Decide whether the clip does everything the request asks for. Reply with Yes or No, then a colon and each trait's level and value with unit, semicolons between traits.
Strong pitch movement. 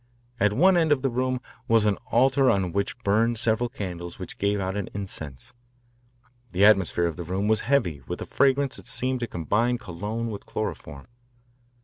No: average, 4.8 semitones